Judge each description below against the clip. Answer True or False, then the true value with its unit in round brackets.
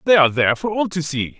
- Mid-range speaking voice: True (160 Hz)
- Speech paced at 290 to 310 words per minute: True (300 wpm)